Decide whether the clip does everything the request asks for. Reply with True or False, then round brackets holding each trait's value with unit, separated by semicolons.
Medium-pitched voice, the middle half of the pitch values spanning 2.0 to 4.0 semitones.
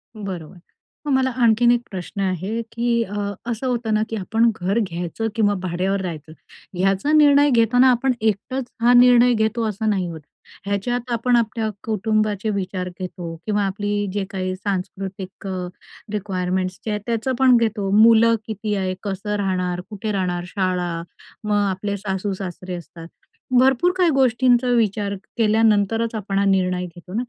False (205 Hz; 3.6 semitones)